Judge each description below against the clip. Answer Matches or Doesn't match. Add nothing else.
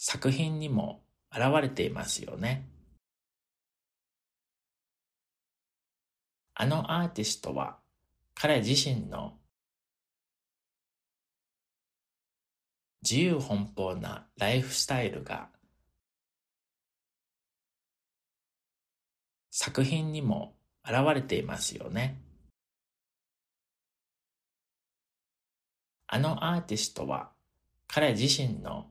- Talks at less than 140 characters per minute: Matches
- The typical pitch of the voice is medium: Doesn't match